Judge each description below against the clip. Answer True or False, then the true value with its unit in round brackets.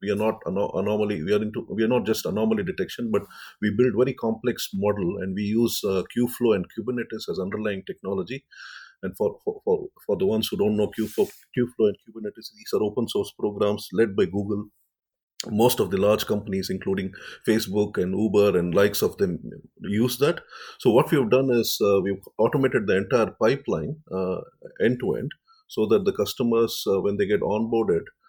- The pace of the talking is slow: False (195 wpm)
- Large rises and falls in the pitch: False (3.9 semitones)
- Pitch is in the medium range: False (110 Hz)